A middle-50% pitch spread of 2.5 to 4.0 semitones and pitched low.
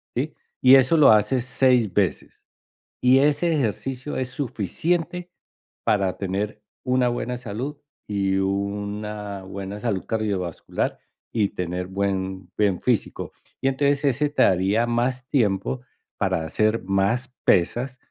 No: average, 4.8 semitones; low, 110 Hz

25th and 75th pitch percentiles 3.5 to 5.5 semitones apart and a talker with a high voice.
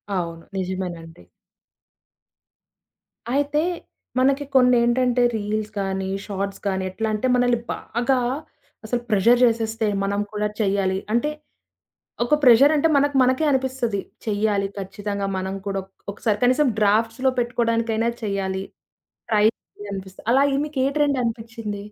Yes: average, 4.1 semitones; high, 220 Hz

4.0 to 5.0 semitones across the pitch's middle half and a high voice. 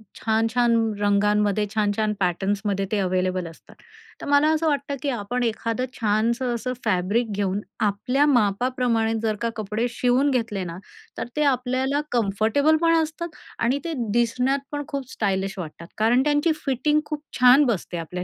Yes: average, 4.6 semitones; high, 230 Hz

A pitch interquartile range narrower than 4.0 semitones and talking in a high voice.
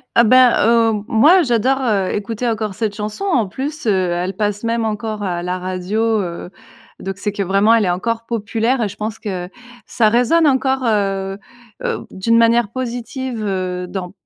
Yes: average, 3.3 semitones; high, 215 Hz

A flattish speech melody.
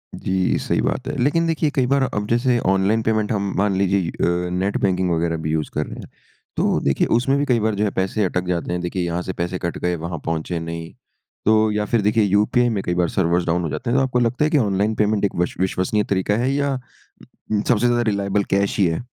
No: average, 4.5 semitones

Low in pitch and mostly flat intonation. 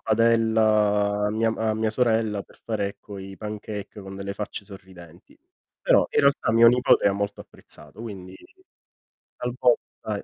Yes: low, 105 Hz; narrow, 2.1 semitones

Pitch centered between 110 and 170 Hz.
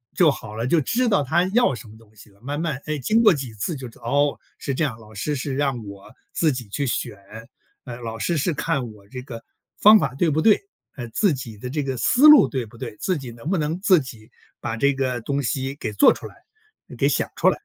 Yes: low, 135 Hz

